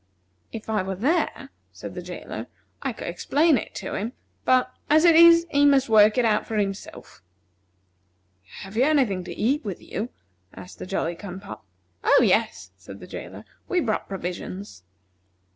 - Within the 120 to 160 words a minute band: No, average, 175 wpm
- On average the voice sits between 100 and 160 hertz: No, high, 215 Hz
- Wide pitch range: Yes, wide, 6.6 semitones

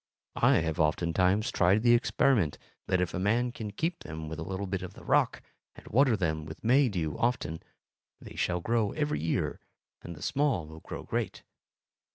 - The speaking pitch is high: No, very low, 95 Hz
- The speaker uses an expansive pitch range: Yes, wide, 6.7 semitones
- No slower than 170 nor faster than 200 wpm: Yes, average, 180 wpm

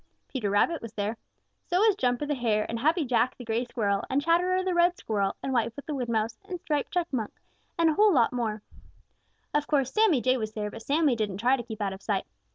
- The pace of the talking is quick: Yes, fast, 225 wpm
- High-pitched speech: Yes, very high, 250 Hz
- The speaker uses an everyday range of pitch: No, wide, 6.3 semitones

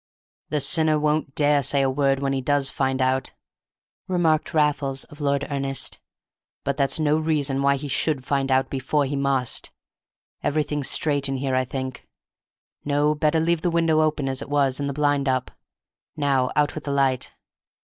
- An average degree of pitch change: No, narrow, 1.9 semitones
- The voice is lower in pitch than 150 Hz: Yes, medium, 140 Hz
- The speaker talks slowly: No, average, 180 wpm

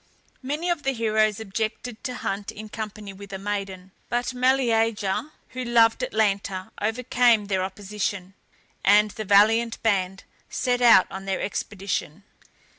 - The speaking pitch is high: Yes, high, 215 Hz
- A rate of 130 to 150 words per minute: Yes, slow, 135 wpm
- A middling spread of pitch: Yes, average, 3.2 semitones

